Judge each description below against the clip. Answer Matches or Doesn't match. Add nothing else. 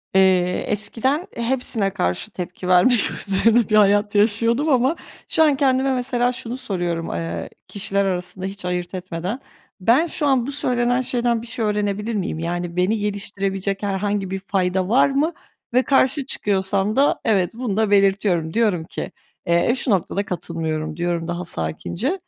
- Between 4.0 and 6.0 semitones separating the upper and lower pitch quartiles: Matches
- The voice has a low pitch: Doesn't match